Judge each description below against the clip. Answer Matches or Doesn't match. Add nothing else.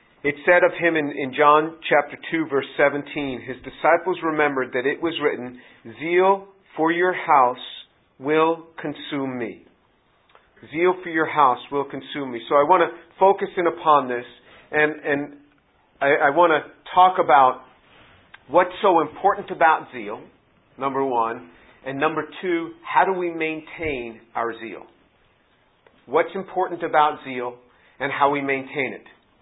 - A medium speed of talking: Matches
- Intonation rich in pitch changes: Doesn't match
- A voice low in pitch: Doesn't match